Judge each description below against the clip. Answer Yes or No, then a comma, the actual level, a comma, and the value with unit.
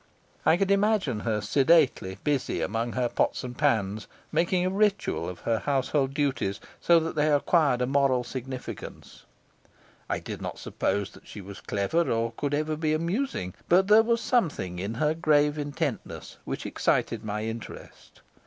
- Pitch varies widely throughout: Yes, wide, 6.5 semitones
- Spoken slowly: No, average, 160 wpm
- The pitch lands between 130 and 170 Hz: Yes, medium, 140 Hz